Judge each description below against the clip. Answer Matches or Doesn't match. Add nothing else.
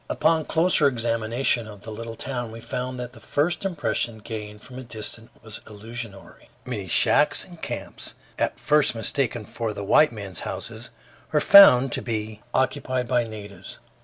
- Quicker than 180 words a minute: Doesn't match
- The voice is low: Matches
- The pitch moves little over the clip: Doesn't match